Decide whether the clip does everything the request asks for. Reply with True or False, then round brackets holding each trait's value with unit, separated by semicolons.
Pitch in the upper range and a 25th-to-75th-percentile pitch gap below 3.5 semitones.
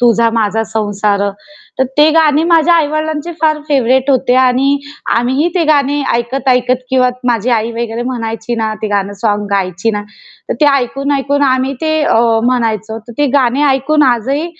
False (255 Hz; 4.0 semitones)